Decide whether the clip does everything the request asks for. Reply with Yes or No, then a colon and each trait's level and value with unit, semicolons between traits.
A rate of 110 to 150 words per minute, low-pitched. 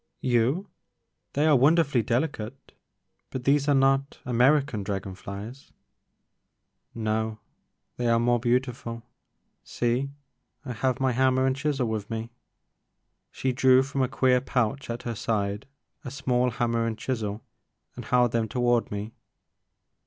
Yes: average, 145 wpm; low, 125 Hz